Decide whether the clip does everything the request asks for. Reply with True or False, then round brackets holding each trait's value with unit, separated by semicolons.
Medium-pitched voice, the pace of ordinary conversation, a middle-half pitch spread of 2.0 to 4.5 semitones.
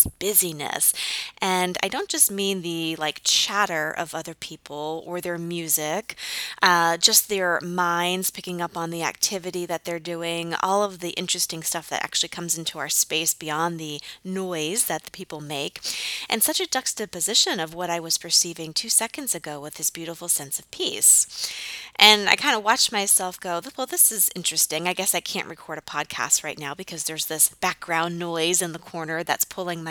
True (175 Hz; 190 wpm; 2.8 semitones)